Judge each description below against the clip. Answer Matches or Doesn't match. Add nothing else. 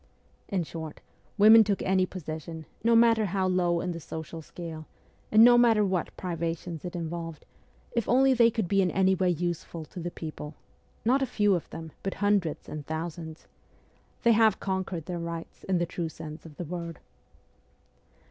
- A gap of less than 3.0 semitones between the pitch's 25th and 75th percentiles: Doesn't match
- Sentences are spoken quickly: Doesn't match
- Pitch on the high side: Doesn't match